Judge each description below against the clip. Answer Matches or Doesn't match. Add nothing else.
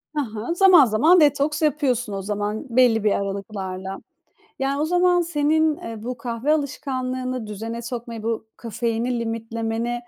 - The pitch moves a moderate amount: Matches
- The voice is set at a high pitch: Matches